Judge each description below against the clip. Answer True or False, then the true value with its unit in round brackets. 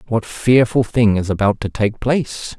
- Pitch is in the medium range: False (110 Hz)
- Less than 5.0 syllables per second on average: True (4.6 syllables/s)